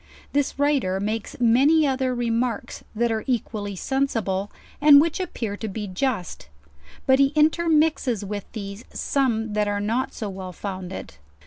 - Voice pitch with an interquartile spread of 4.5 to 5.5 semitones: Yes, average, 5.1 semitones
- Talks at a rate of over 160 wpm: No, average, 155 wpm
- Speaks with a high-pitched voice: Yes, high, 230 Hz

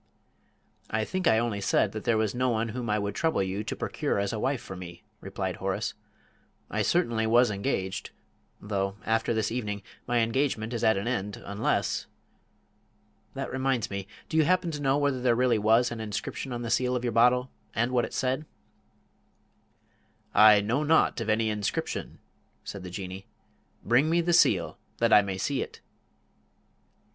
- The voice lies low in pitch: Yes, low, 115 Hz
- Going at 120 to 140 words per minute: No, average, 180 wpm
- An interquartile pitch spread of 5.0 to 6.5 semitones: No, average, 3.6 semitones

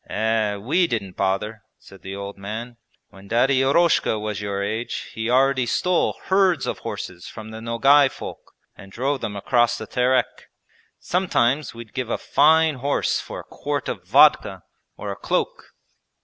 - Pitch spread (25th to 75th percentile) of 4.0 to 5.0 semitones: Yes, average, 4.7 semitones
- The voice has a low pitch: Yes, low, 115 Hz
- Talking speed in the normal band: Yes, average, 165 wpm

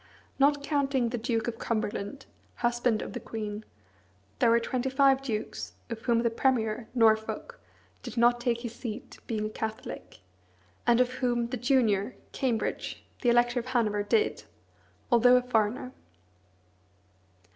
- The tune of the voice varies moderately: No, narrow, 2.3 semitones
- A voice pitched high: Yes, high, 240 Hz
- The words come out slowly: No, average, 145 wpm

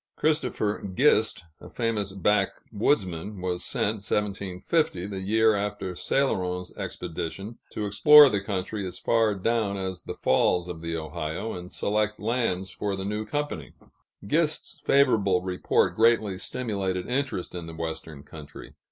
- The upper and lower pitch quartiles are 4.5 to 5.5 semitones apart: No, average, 3.5 semitones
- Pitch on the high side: No, low, 100 Hz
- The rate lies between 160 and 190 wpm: No, slow, 135 wpm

